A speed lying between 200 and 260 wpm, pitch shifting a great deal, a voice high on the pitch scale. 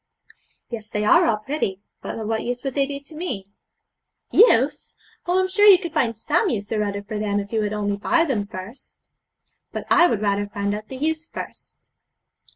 Yes: fast, 205 wpm; wide, 7.0 semitones; high, 225 Hz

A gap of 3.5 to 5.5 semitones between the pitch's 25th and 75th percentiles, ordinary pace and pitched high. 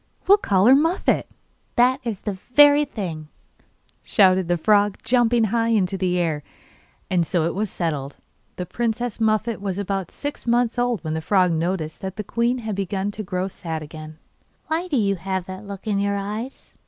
Yes: average, 4.5 semitones; average, 190 wpm; high, 200 Hz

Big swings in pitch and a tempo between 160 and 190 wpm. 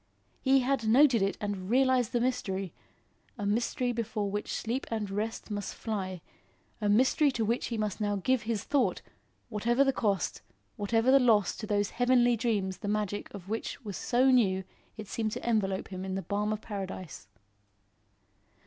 No: average, 3.1 semitones; average, 175 wpm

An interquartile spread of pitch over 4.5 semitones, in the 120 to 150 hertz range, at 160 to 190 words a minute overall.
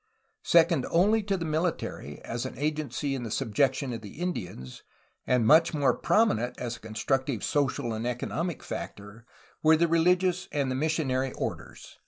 Yes: wide, 5.6 semitones; medium, 140 Hz; average, 165 wpm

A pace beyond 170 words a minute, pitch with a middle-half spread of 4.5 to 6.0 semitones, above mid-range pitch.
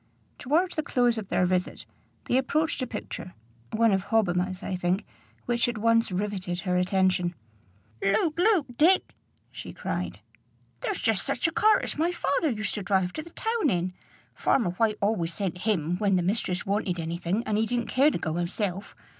Yes: average, 185 wpm; wide, 5.5 semitones; high, 210 Hz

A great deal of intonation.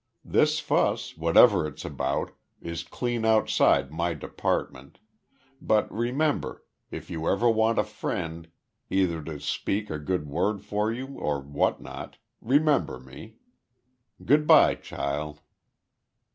Yes: wide, 6.6 semitones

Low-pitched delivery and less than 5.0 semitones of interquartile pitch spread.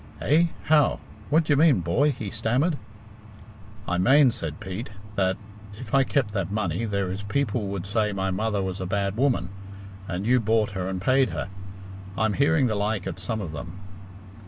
No: low, 105 Hz; average, 5.3 semitones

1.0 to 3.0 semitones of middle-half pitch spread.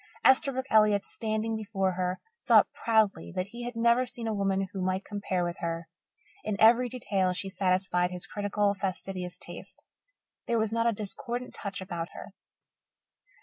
No: average, 3.4 semitones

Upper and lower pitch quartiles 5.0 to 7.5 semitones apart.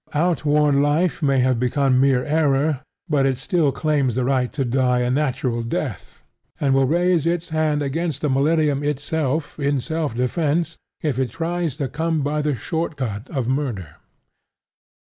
No: average, 3.3 semitones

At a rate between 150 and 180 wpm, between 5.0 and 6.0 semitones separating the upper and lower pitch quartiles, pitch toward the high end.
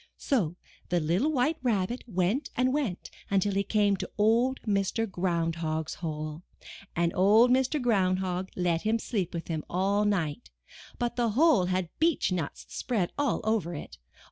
Yes: average, 165 wpm; average, 5.3 semitones; high, 195 Hz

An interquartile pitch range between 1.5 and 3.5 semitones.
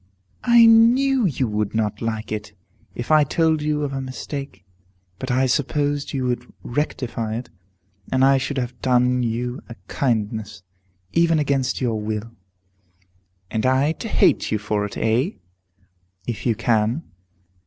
No: average, 4.5 semitones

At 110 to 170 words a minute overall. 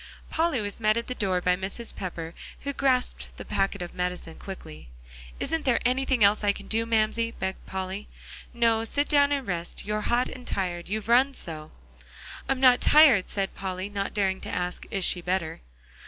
No: average, 185 wpm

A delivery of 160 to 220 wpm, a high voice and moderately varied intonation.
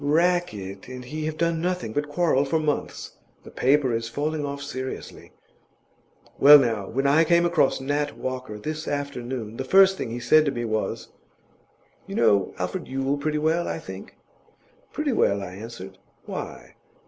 No: average, 165 wpm; medium, 140 Hz; average, 4.7 semitones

